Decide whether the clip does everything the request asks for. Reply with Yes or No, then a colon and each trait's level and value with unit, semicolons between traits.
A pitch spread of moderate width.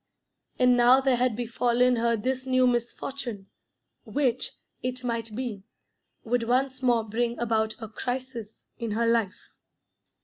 No: narrow, 1.8 semitones